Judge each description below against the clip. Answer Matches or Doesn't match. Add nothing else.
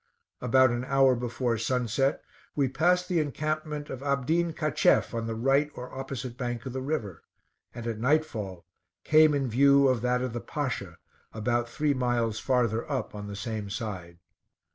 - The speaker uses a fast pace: Doesn't match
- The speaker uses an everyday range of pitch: Matches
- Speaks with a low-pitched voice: Matches